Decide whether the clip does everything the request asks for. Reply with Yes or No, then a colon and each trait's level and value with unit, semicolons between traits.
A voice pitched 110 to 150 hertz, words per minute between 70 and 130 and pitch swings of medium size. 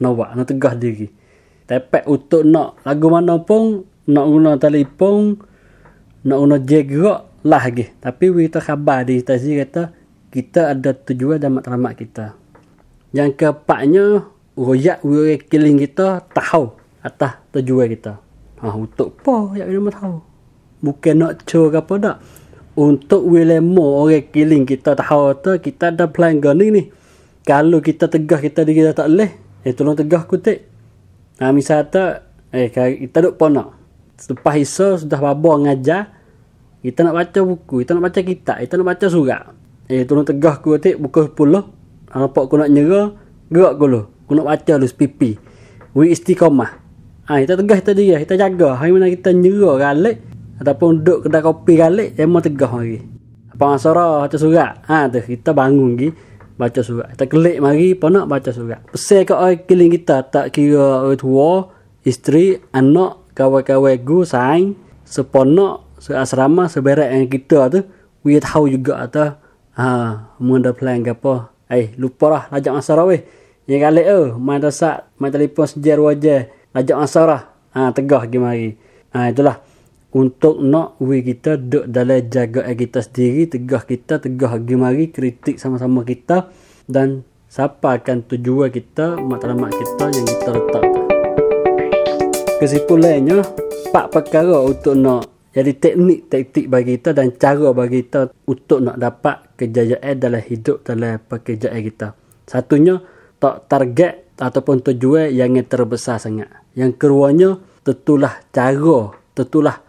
No: medium, 140 Hz; fast, 155 wpm; average, 4.4 semitones